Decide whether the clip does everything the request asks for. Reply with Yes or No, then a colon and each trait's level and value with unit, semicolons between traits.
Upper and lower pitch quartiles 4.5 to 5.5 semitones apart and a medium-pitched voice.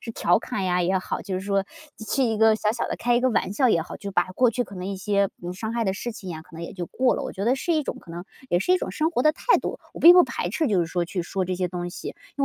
No: average, 5.1 semitones; high, 200 Hz